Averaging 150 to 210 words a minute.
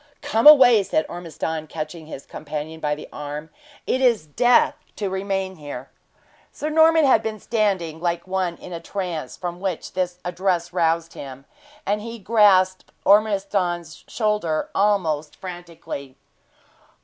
No: slow, 135 wpm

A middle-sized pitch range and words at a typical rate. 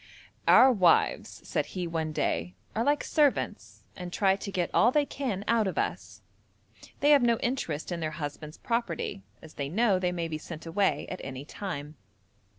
No: wide, 6.8 semitones; average, 180 wpm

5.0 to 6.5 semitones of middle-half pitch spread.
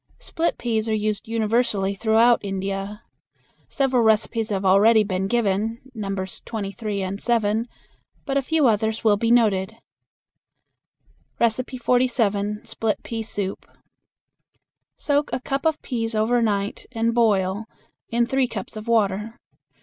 No: average, 2.8 semitones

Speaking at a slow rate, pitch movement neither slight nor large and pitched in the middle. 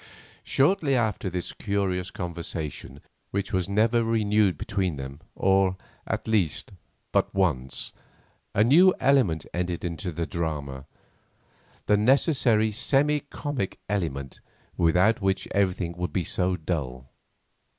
No: slow, 120 wpm; average, 4.6 semitones; very low, 95 Hz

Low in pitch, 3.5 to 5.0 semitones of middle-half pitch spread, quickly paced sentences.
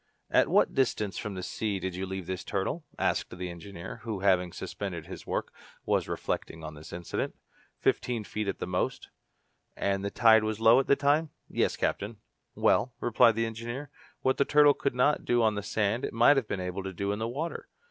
Yes: low, 105 Hz; average, 4.0 semitones; fast, 215 wpm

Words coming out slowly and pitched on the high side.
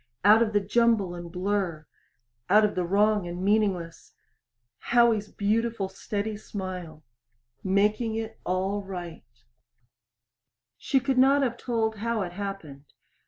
Yes: slow, 125 wpm; high, 205 Hz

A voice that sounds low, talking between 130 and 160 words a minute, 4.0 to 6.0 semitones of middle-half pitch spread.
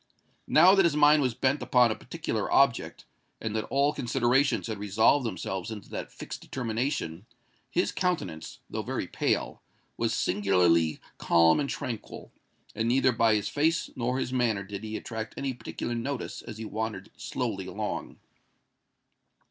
Yes: low, 115 Hz; average, 155 wpm; average, 4.4 semitones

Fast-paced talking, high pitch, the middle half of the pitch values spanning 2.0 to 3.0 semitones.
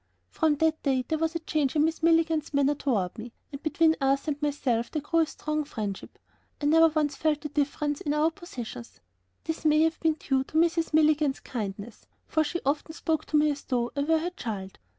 Yes: fast, 210 wpm; very high, 300 Hz; average, 2.7 semitones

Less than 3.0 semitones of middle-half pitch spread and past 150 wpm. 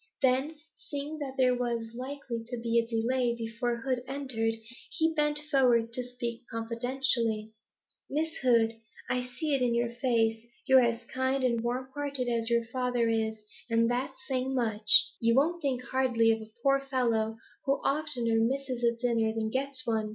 Yes: narrow, 2.5 semitones; average, 170 wpm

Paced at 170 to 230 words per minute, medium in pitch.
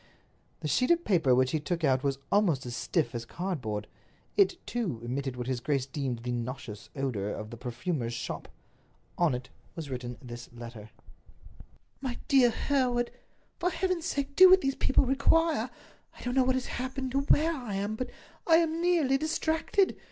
Yes: average, 175 wpm; medium, 180 Hz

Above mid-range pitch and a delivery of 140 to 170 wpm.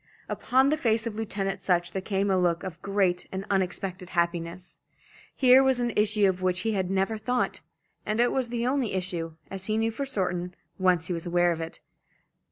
No: high, 195 Hz; average, 200 wpm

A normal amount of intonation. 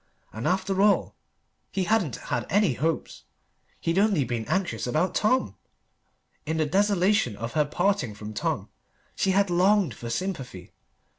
No: wide, 8.1 semitones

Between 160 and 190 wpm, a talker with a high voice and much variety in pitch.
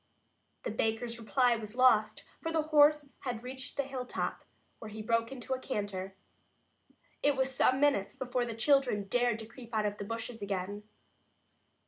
No: average, 165 wpm; high, 235 Hz; average, 3.6 semitones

